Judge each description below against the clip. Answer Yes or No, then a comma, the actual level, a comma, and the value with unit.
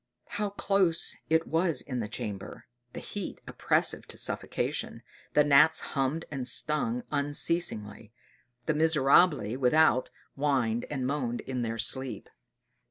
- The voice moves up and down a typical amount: Yes, average, 4.5 semitones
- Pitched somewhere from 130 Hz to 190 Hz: Yes, medium, 140 Hz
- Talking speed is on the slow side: Yes, slow, 125 wpm